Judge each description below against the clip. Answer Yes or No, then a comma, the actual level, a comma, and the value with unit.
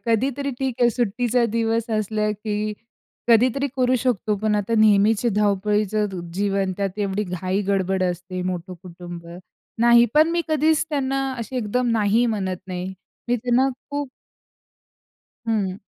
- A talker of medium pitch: No, high, 215 Hz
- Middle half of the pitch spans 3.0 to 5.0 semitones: Yes, average, 3.9 semitones